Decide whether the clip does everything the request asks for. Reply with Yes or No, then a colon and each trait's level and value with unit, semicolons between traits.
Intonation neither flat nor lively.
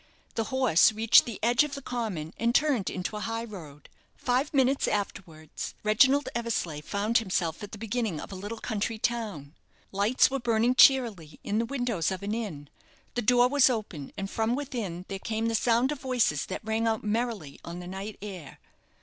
Yes: average, 4.2 semitones